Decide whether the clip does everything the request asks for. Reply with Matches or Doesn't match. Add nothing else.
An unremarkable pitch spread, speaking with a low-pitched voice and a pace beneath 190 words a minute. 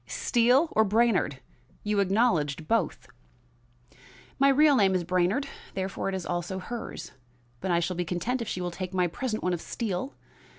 Doesn't match